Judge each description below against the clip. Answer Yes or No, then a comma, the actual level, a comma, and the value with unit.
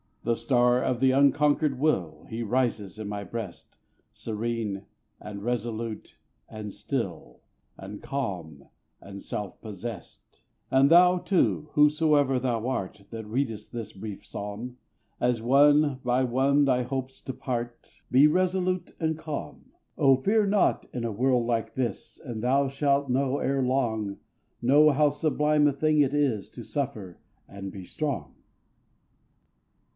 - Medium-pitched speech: No, low, 125 Hz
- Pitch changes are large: No, average, 4.6 semitones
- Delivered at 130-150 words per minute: Yes, average, 140 wpm